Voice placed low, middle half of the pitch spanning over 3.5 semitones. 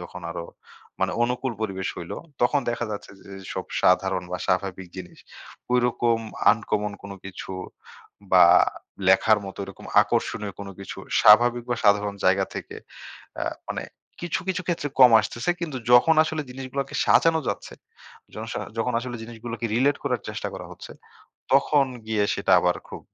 Yes: low, 110 Hz; average, 4.5 semitones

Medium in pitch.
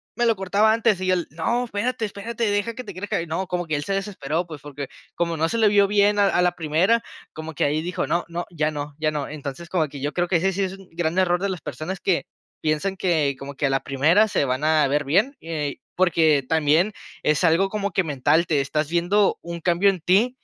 Yes: medium, 175 Hz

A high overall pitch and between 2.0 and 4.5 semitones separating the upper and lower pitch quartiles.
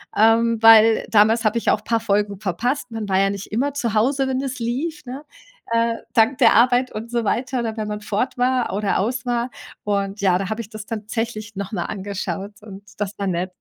Yes: high, 220 Hz; average, 2.9 semitones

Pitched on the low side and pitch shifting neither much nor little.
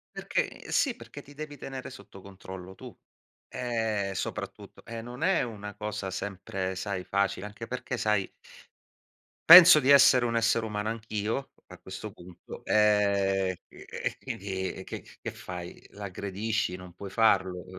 Yes: low, 105 Hz; average, 3.4 semitones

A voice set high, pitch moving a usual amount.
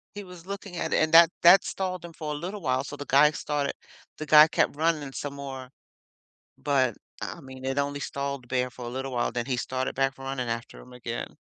No: medium, 140 Hz; average, 3.3 semitones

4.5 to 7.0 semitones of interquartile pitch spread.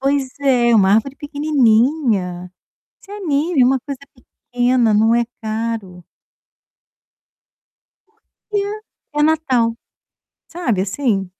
Yes: average, 4.8 semitones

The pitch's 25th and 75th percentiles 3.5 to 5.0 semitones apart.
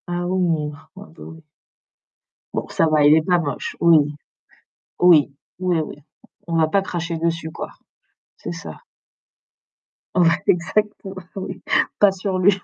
No: average, 2.7 semitones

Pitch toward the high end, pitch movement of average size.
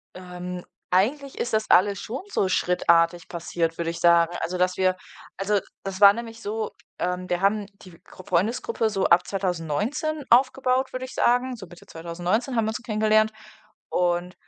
Yes: high, 195 Hz; average, 4.2 semitones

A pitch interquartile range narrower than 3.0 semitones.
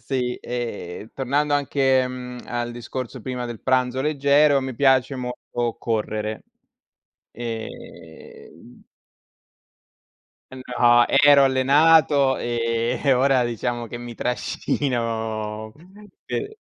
Yes: narrow, 2.4 semitones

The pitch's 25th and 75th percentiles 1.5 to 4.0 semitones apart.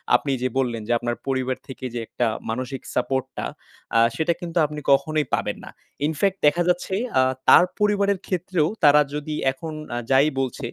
No: average, 4.7 semitones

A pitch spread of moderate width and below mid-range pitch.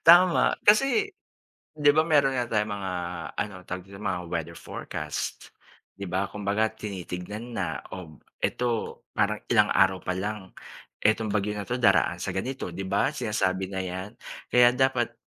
Yes: average, 4.4 semitones; low, 105 Hz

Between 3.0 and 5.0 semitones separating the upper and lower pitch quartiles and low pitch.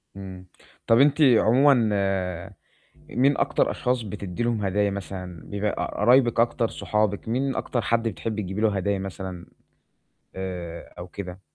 Yes: average, 3.9 semitones; low, 105 Hz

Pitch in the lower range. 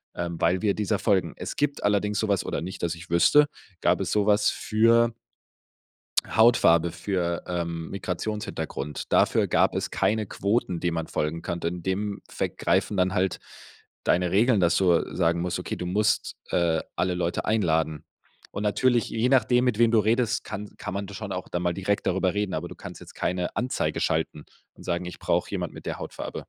Yes: very low, 95 Hz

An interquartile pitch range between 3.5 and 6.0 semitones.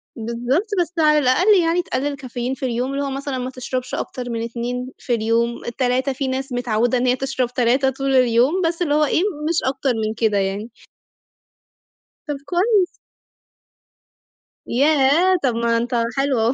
No: average, 3.0 semitones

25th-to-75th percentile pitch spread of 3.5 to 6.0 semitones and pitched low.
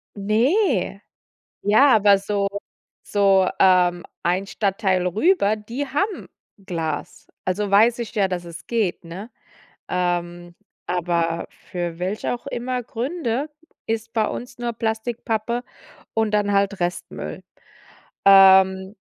No: average, 4.0 semitones; high, 200 Hz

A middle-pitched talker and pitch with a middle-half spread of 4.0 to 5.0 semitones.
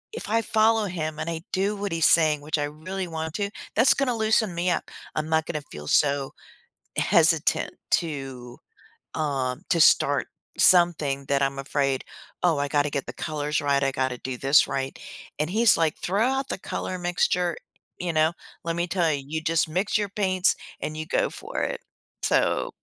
Yes: medium, 160 Hz; average, 4.4 semitones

